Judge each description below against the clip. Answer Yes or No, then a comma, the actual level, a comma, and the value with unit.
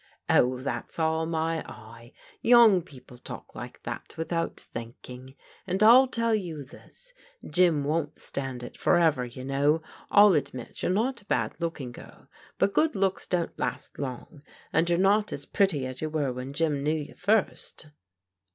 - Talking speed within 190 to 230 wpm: No, average, 170 wpm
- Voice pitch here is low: No, medium, 160 Hz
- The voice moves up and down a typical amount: No, wide, 6.1 semitones